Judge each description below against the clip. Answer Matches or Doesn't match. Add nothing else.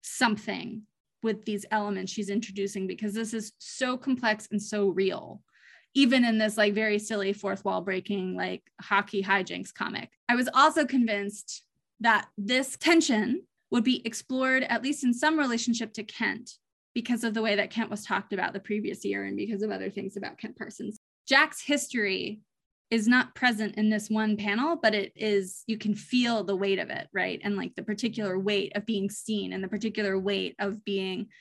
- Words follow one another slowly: Doesn't match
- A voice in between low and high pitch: Doesn't match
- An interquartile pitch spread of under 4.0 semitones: Matches